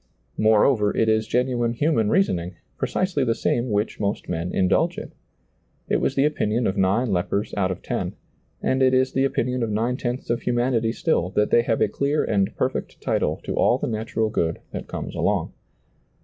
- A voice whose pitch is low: Yes, low, 115 Hz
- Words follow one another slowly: No, average, 190 wpm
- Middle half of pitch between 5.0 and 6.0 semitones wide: No, average, 3.8 semitones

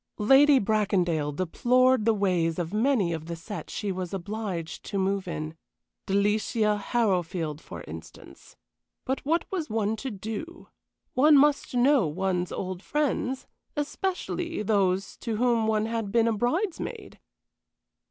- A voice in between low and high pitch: No, high, 210 Hz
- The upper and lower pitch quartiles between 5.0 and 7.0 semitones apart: Yes, wide, 5.6 semitones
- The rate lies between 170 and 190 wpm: No, slow, 135 wpm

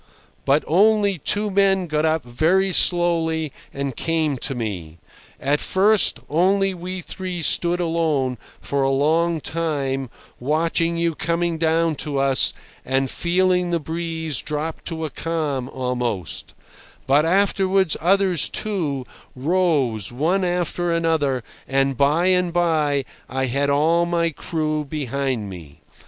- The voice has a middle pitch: Yes, medium, 160 Hz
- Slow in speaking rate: Yes, slow, 130 wpm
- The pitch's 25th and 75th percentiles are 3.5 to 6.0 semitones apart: Yes, average, 4.1 semitones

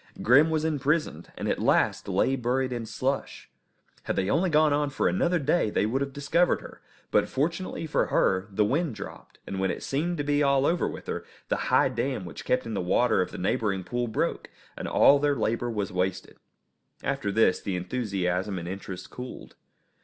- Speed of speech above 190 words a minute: Yes, average, 200 wpm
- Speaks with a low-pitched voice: Yes, low, 125 Hz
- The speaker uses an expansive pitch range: Yes, wide, 6.7 semitones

